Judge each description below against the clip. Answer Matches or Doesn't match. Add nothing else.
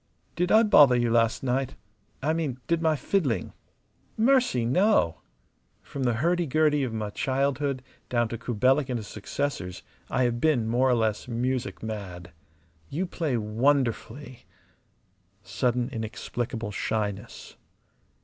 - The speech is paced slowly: Matches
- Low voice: Matches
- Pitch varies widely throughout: Doesn't match